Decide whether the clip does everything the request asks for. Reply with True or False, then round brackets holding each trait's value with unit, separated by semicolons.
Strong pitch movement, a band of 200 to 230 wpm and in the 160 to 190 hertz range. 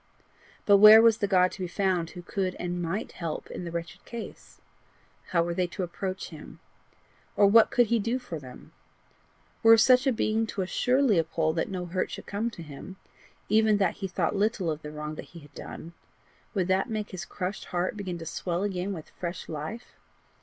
False (3.8 semitones; 205 wpm; 185 Hz)